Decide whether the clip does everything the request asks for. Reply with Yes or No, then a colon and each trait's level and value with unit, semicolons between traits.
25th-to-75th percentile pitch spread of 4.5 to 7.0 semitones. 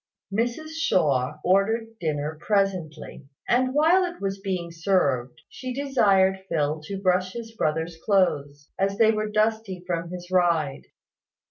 Yes: wide, 5.4 semitones